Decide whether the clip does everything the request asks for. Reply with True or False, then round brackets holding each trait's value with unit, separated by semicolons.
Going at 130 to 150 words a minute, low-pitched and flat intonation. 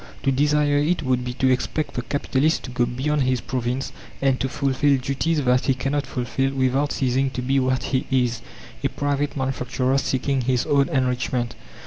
False (180 wpm; 130 Hz; 1.7 semitones)